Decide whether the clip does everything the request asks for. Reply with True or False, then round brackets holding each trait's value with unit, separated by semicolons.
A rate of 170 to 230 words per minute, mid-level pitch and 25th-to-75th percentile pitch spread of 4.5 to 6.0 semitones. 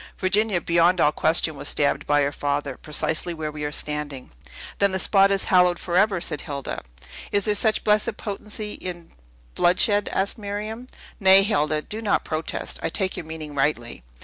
True (175 wpm; 175 Hz; 5.1 semitones)